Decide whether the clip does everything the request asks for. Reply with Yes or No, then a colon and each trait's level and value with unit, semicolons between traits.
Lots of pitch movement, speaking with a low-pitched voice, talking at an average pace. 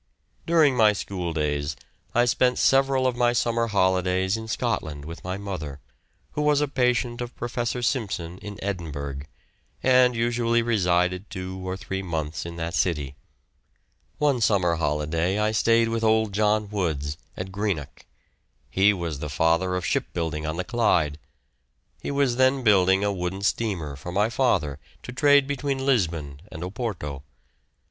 Yes: wide, 6.1 semitones; low, 100 Hz; average, 155 wpm